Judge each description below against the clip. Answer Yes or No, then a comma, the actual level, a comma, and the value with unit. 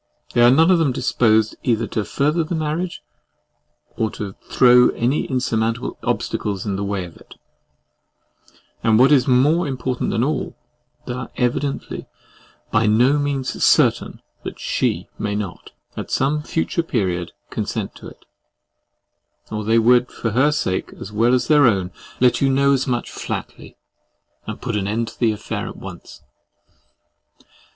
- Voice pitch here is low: Yes, low, 125 Hz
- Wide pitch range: No, average, 4.2 semitones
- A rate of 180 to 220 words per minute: No, average, 155 wpm